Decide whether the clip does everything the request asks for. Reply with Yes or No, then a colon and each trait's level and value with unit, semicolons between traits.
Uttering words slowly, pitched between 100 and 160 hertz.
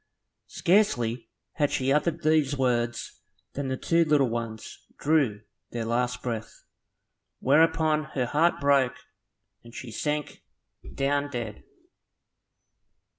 Yes: slow, 110 wpm; low, 135 Hz